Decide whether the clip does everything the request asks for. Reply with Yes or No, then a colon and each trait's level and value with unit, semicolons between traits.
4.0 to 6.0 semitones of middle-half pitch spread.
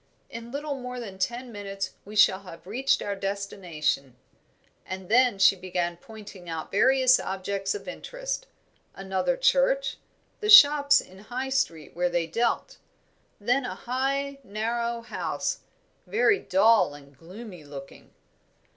Yes: wide, 5.6 semitones